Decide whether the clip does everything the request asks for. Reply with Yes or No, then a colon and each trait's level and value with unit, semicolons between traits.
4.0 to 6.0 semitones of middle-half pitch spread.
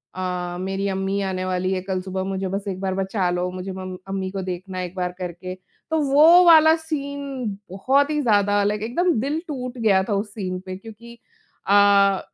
Yes: average, 4.7 semitones